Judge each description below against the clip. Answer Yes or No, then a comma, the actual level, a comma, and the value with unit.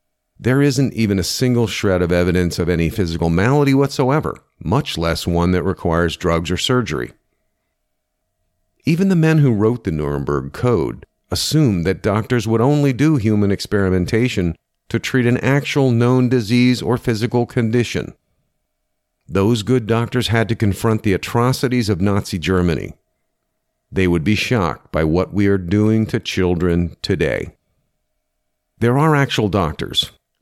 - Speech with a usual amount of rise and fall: No, wide, 5.8 semitones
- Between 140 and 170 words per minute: Yes, average, 145 wpm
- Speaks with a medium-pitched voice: No, low, 105 Hz